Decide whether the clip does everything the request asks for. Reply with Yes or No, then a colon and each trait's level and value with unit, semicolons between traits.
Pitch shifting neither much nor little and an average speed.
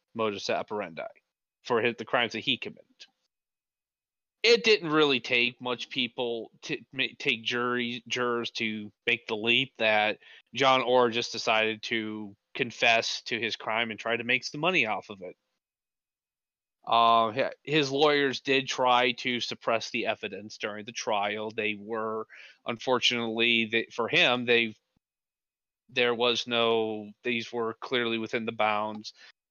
No: narrow, 2.0 semitones; average, 145 wpm